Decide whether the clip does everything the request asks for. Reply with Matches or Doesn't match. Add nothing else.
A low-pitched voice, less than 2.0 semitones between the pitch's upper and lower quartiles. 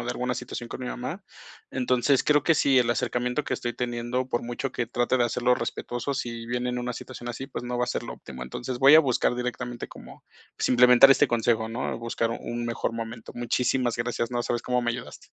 Matches